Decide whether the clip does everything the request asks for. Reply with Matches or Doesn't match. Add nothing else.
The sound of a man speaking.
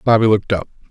Matches